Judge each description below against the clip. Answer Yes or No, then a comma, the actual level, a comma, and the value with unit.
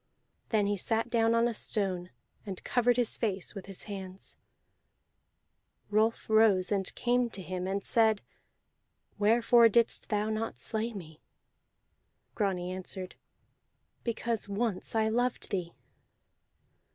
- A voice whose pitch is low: No, high, 215 Hz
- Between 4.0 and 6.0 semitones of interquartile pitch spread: No, average, 3.1 semitones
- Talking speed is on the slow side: Yes, slow, 125 wpm